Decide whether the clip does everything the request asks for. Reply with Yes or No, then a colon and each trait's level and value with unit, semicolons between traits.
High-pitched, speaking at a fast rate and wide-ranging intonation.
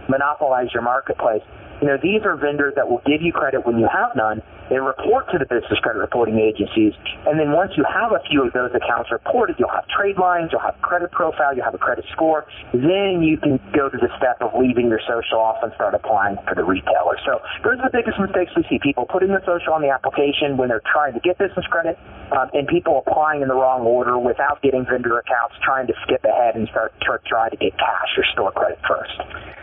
No: medium, 140 Hz; fast, 235 wpm; wide, 6.4 semitones